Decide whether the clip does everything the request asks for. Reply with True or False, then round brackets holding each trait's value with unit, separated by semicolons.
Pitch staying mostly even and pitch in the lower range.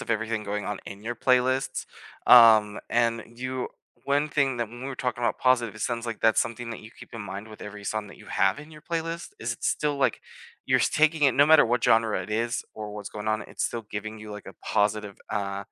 False (3.4 semitones; 115 Hz)